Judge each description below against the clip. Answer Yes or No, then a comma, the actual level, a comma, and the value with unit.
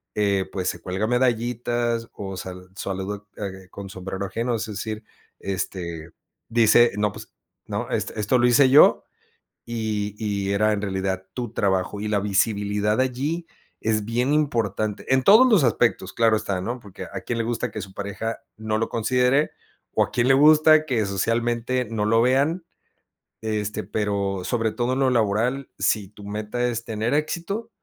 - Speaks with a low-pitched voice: Yes, low, 110 Hz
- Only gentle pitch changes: No, average, 3.3 semitones